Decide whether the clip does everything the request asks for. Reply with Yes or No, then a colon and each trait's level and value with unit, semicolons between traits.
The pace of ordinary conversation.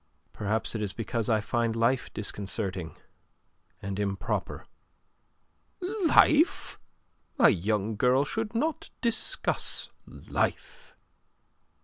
No: slow, 90 wpm